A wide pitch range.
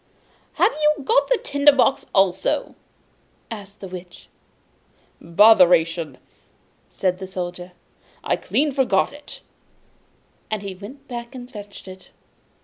Yes: wide, 6.6 semitones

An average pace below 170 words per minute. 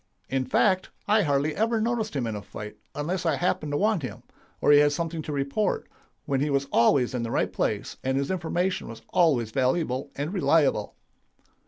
No: average, 195 wpm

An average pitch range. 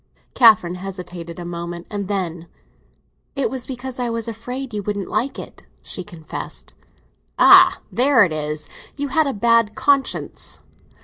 No: wide, 6.3 semitones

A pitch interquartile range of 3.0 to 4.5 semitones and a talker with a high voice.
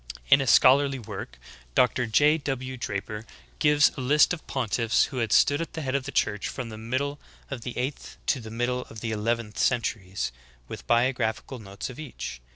No: average, 3.7 semitones; low, 125 Hz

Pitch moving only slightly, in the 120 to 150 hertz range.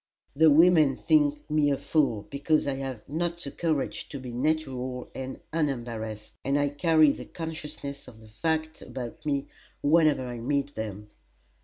No: average, 3.8 semitones; medium, 140 Hz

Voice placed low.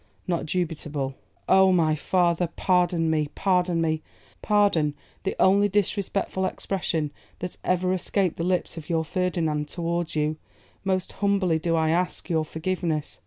No: medium, 175 Hz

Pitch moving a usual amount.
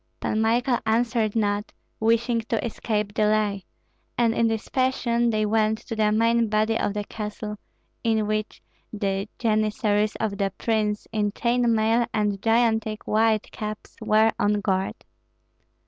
No: narrow, 1.4 semitones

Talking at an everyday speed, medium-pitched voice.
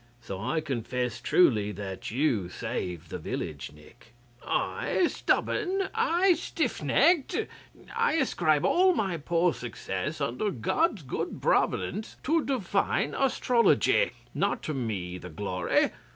No: slow, 125 wpm; medium, 150 Hz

